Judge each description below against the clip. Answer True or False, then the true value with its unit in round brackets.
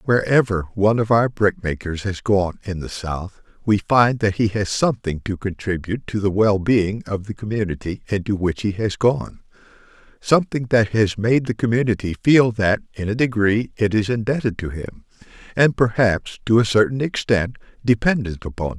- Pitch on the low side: True (105 Hz)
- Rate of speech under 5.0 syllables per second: False (5.1 syllables/s)